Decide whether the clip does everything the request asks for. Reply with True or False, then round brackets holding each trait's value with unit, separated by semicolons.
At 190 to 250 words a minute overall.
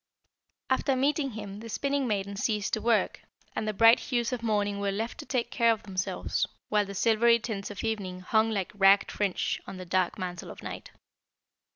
True (195 wpm)